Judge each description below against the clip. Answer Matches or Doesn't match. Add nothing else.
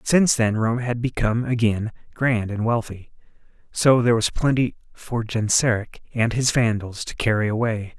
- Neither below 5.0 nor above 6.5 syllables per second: Matches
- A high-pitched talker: Doesn't match